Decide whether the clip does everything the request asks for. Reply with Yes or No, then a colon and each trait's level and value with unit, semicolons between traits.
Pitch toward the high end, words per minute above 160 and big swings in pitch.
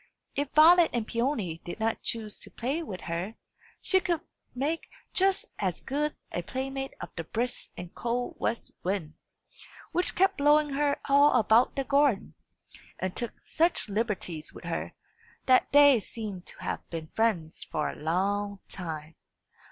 No: high, 235 Hz; average, 155 wpm; wide, 7.3 semitones